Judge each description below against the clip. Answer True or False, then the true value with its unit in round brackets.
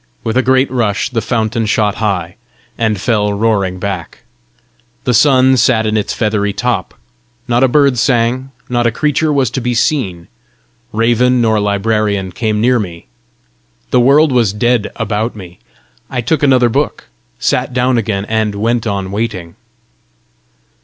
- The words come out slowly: False (155 wpm)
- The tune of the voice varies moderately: True (3.3 semitones)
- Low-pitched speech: True (115 Hz)